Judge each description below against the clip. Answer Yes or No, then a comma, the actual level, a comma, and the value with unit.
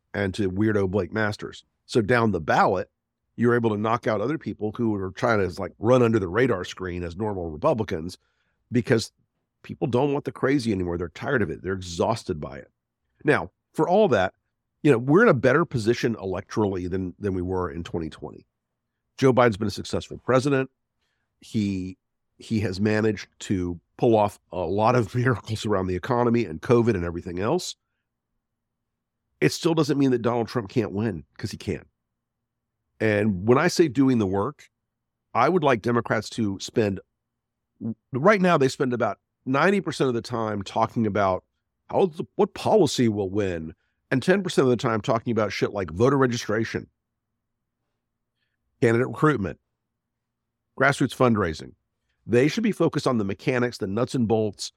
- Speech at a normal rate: Yes, average, 170 wpm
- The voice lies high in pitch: No, low, 110 Hz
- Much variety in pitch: No, average, 4.3 semitones